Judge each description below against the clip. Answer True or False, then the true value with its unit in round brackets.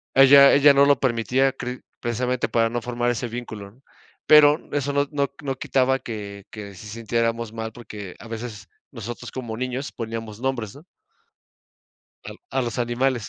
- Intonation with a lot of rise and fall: False (2.8 semitones)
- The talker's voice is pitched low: True (120 Hz)